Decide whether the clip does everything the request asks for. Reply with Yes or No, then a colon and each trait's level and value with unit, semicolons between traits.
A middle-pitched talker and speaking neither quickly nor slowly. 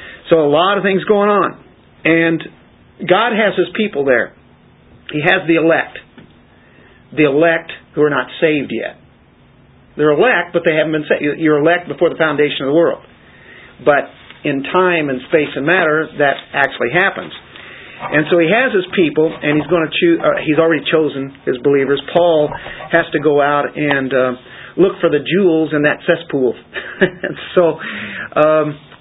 Yes: medium, 155 Hz; average, 170 wpm